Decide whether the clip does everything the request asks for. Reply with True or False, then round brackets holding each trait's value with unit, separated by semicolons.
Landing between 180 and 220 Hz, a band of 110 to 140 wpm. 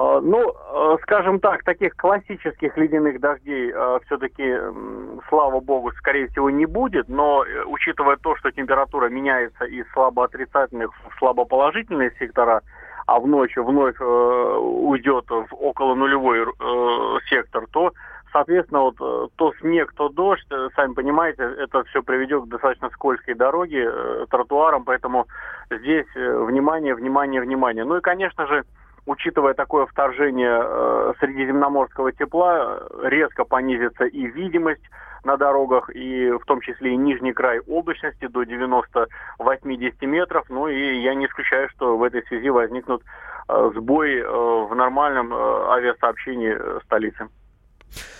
False (135 Hz; 130 wpm)